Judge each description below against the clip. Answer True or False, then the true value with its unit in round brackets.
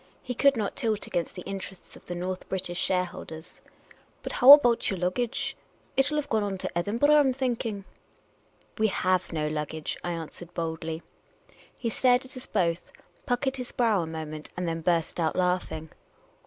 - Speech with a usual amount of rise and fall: False (6.4 semitones)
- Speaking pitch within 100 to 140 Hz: False (185 Hz)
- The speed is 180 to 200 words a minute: True (185 wpm)